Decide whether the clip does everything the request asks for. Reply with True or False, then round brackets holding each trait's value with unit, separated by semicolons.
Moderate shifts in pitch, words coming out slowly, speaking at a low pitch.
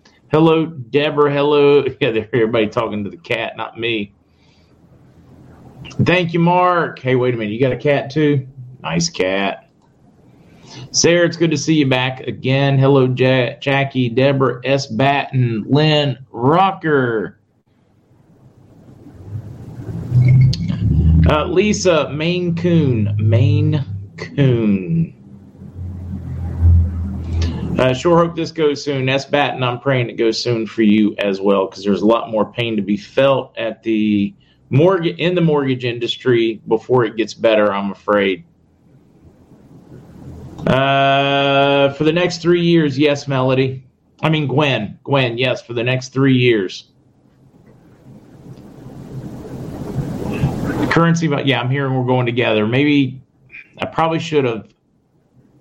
True (4.6 semitones; 130 wpm; 130 Hz)